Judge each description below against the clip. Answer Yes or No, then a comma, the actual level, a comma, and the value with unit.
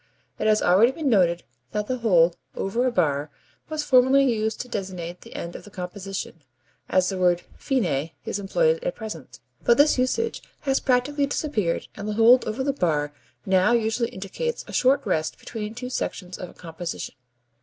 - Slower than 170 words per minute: No, average, 180 wpm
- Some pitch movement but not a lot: No, wide, 6.1 semitones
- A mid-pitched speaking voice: No, high, 215 Hz